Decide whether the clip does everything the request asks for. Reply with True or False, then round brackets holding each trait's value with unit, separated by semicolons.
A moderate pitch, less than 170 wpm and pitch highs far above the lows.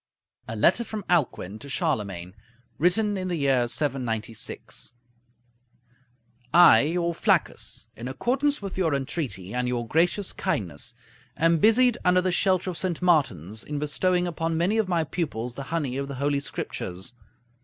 True (155 Hz; 150 wpm; 6.7 semitones)